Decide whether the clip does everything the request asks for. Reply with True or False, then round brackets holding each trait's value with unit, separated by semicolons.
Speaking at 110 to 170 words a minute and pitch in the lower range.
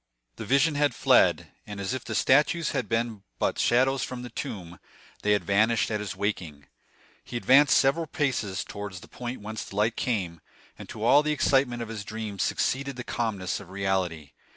False (190 wpm; 110 Hz)